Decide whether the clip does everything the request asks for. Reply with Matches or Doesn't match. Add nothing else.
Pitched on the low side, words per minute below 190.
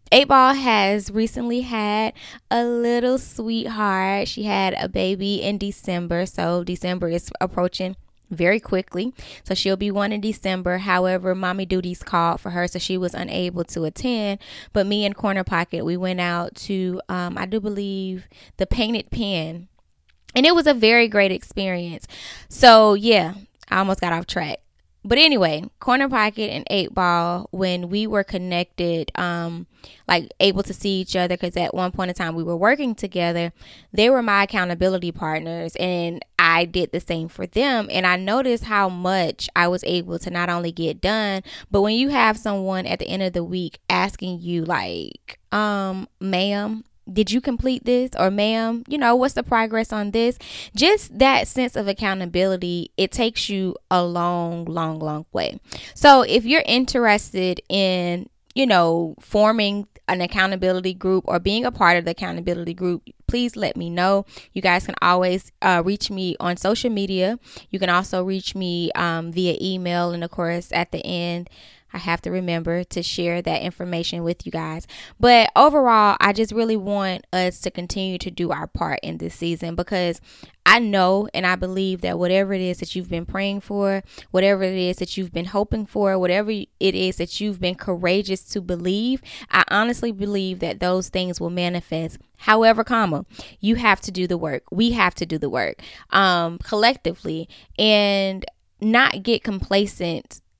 Doesn't match